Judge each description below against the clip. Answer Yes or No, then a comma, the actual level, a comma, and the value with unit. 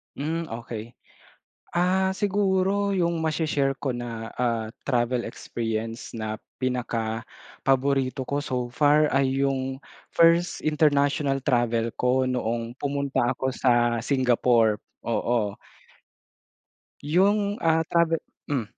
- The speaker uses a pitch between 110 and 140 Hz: Yes, low, 135 Hz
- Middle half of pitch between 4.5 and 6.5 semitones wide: Yes, average, 4.8 semitones